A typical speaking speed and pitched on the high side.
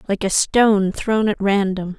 Yes: average, 180 wpm; high, 200 Hz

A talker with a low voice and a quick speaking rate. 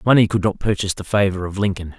Yes: low, 100 Hz; fast, 240 wpm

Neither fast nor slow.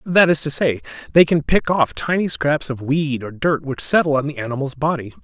No: fast, 230 wpm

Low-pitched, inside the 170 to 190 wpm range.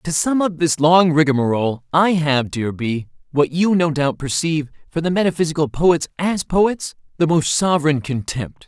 No: medium, 160 Hz; average, 175 wpm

